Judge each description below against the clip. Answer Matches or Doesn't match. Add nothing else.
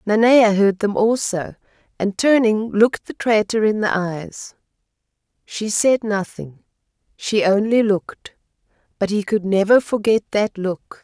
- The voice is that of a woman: Matches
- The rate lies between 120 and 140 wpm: Matches